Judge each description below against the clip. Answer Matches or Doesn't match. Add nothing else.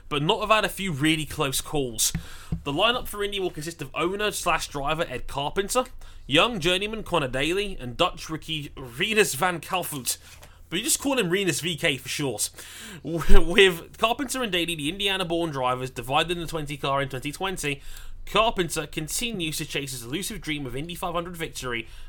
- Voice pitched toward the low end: Doesn't match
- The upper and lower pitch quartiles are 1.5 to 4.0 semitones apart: Doesn't match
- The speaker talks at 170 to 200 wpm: Matches